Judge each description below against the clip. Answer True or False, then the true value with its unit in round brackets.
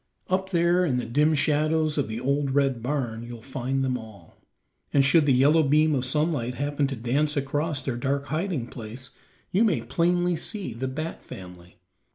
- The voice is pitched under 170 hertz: True (140 Hz)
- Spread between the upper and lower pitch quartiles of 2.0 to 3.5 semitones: False (3.9 semitones)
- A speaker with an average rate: True (185 wpm)